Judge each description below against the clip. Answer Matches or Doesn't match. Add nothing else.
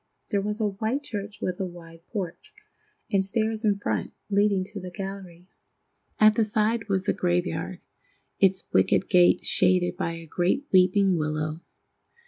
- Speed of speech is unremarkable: Matches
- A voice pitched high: Matches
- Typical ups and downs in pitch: Matches